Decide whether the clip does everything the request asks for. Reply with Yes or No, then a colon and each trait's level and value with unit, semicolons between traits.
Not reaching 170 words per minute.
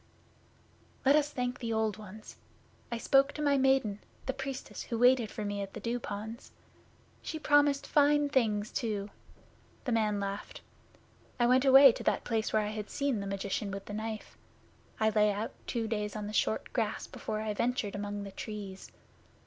No: average, 180 wpm